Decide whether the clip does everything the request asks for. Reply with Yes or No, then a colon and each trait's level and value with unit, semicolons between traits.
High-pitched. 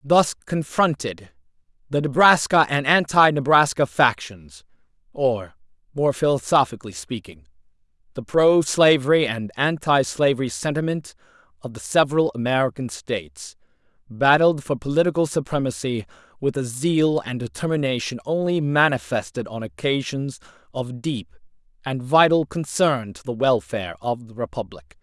No: low, 135 Hz